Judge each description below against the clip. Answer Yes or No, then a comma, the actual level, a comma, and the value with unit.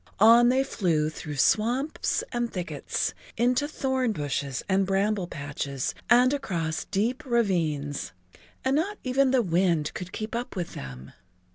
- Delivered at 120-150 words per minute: Yes, average, 140 wpm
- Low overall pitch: No, high, 200 Hz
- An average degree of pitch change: No, wide, 7.9 semitones